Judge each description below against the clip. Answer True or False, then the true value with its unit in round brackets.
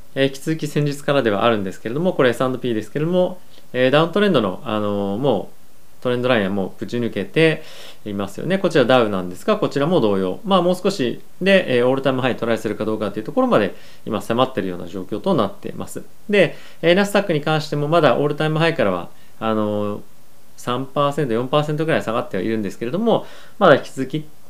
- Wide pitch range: True (6.5 semitones)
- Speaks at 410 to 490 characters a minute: True (430 characters per minute)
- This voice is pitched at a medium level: False (130 Hz)